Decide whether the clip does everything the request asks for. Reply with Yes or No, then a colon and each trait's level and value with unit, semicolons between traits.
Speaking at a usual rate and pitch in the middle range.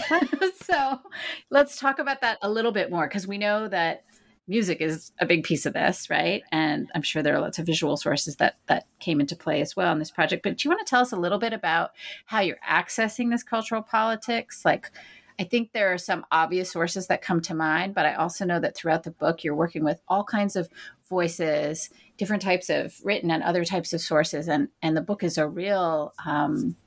No: fast, 225 wpm; medium, 180 Hz